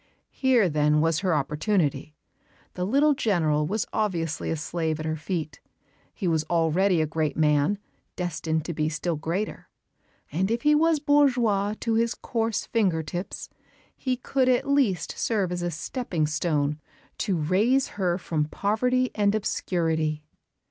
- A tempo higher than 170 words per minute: No, average, 150 wpm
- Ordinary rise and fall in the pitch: No, wide, 6.1 semitones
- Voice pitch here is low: No, medium, 175 Hz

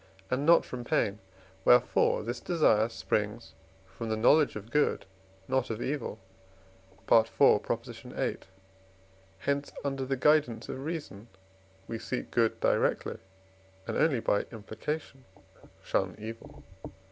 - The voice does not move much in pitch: No, average, 4.3 semitones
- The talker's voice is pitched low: Yes, low, 120 Hz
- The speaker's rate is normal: No, slow, 120 wpm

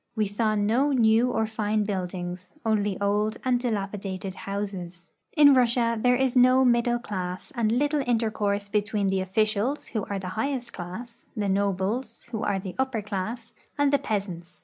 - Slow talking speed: No, average, 175 wpm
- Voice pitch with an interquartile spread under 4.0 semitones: Yes, average, 3.4 semitones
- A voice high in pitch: Yes, high, 215 Hz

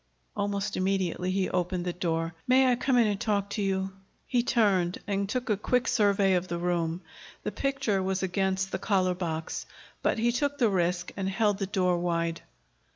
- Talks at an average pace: Yes, average, 190 wpm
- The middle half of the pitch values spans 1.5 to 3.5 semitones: Yes, average, 2.9 semitones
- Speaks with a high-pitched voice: Yes, high, 195 Hz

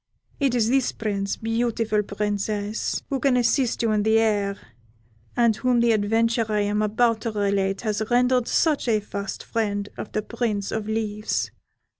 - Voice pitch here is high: Yes, high, 220 Hz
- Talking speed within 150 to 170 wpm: Yes, average, 165 wpm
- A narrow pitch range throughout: Yes, narrow, 2.2 semitones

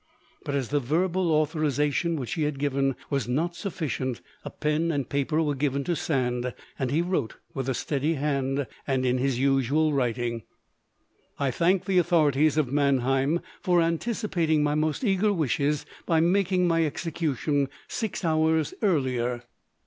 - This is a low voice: No, medium, 150 Hz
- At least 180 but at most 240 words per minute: No, average, 155 wpm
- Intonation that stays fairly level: No, average, 3.6 semitones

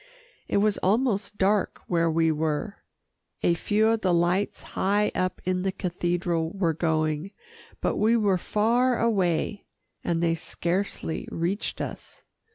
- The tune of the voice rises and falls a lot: No, average, 3.6 semitones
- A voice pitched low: No, medium, 185 Hz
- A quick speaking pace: No, average, 140 wpm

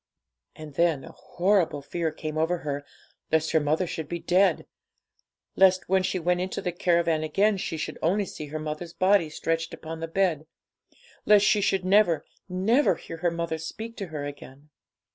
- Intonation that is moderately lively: Yes, average, 3.1 semitones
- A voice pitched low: No, medium, 170 Hz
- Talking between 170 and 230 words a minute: Yes, average, 180 wpm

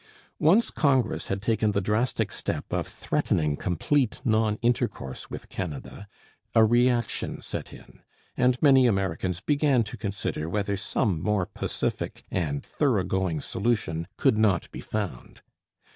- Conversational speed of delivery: No, slow, 130 wpm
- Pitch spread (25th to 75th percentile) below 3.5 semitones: No, average, 4.7 semitones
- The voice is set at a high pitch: No, low, 105 Hz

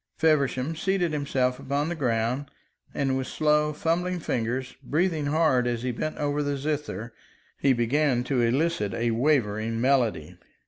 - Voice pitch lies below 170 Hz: Yes, medium, 140 Hz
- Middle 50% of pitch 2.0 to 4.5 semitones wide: Yes, average, 3.9 semitones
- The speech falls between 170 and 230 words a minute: No, average, 145 wpm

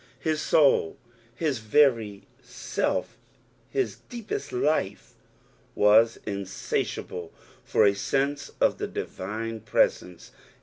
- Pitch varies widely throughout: Yes, wide, 6.1 semitones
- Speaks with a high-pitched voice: No, low, 115 Hz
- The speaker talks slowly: Yes, slow, 95 wpm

